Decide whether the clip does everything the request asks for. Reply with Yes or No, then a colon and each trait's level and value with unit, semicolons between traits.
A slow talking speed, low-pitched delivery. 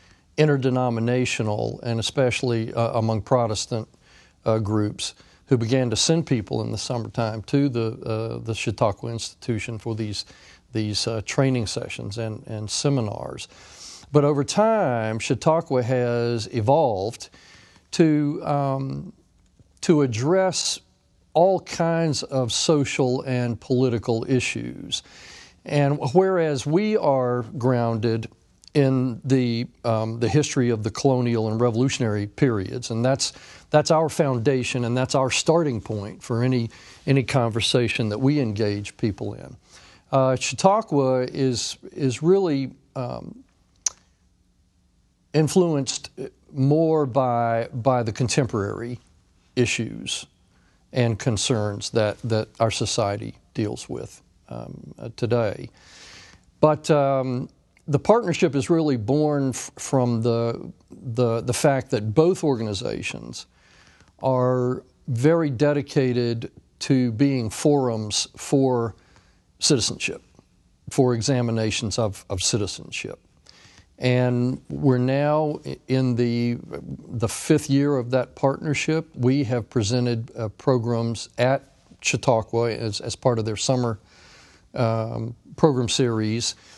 Yes: slow, 115 wpm; low, 125 Hz